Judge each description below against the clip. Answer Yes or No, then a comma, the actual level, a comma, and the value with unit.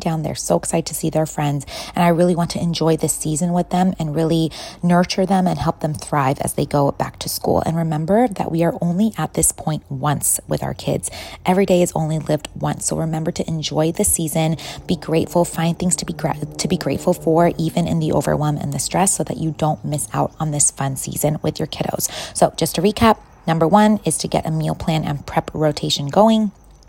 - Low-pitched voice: No, medium, 160 Hz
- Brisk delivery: Yes, fast, 230 wpm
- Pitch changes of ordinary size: No, narrow, 2.3 semitones